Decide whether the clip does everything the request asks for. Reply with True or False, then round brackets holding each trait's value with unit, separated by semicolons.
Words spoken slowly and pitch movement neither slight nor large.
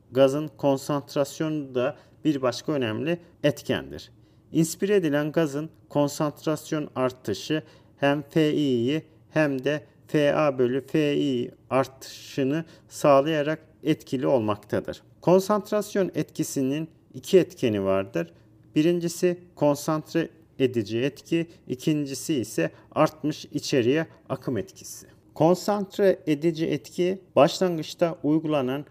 True (90 wpm; 3.4 semitones)